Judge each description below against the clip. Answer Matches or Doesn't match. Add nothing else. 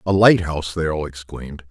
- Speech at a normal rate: Matches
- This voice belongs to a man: Matches